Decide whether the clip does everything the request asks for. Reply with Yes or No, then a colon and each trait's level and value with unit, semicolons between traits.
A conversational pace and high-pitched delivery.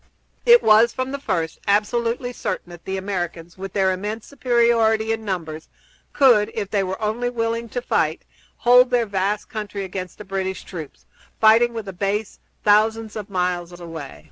Yes: average, 170 wpm; high, 210 Hz